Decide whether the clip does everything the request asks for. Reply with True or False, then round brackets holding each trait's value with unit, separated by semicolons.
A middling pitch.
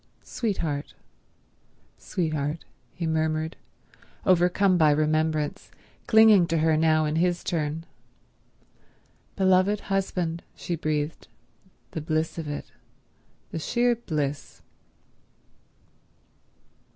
True (160 Hz)